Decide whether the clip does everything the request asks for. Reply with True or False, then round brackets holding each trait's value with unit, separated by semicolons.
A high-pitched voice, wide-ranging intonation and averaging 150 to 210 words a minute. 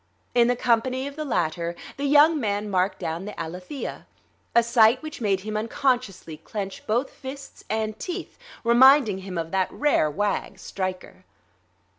True (220 Hz; 5.7 semitones; 155 wpm)